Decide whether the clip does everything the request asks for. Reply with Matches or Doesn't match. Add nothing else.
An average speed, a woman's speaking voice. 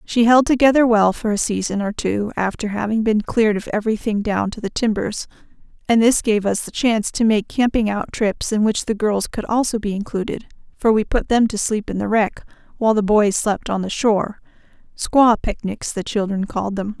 Doesn't match